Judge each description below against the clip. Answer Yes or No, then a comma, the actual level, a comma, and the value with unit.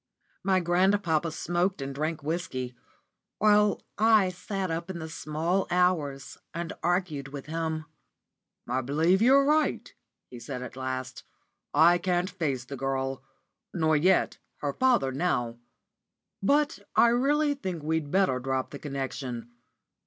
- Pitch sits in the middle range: Yes, medium, 165 Hz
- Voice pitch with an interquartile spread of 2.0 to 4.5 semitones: No, wide, 5.5 semitones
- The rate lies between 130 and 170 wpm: Yes, slow, 135 wpm